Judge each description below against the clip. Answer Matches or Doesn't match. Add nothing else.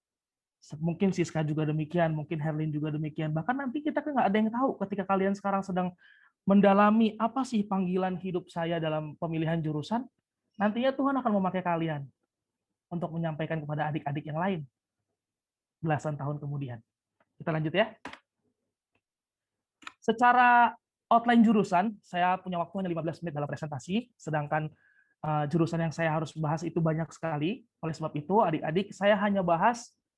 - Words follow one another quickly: Matches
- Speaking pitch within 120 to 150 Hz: Doesn't match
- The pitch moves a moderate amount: Matches